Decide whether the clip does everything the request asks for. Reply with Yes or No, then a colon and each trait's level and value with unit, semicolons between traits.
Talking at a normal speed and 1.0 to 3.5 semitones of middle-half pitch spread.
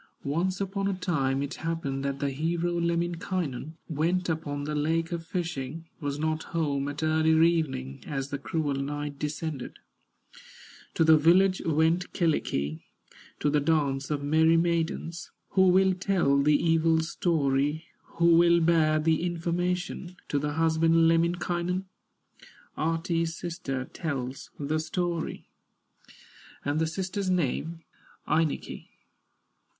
No: slow, 125 wpm; average, 2.8 semitones